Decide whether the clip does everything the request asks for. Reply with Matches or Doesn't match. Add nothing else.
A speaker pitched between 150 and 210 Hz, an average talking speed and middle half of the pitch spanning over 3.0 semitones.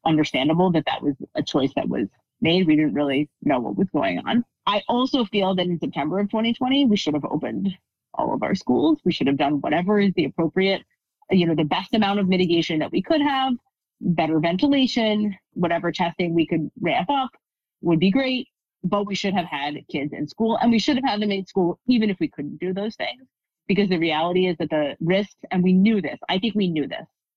Doesn't match